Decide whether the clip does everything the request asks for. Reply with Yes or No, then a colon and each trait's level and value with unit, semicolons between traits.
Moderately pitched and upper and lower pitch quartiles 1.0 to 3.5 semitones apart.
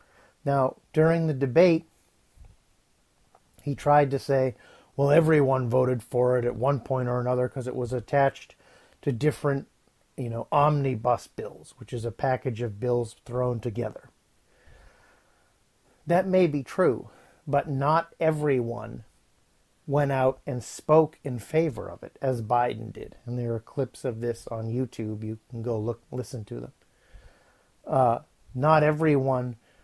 No: low, 130 Hz; average, 3.1 semitones